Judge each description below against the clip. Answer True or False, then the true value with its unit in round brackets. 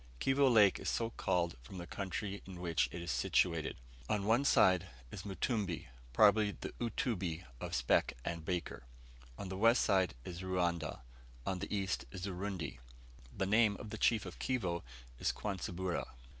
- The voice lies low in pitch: True (95 Hz)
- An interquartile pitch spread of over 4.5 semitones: False (3.3 semitones)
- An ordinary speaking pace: True (160 wpm)